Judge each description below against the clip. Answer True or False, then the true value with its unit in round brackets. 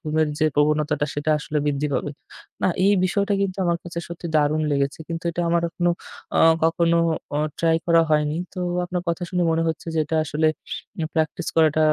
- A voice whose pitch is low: False (160 Hz)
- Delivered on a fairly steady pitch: True (2.1 semitones)